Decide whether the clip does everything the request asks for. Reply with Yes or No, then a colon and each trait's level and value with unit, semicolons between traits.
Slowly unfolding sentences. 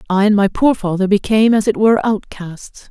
No: fast, 205 wpm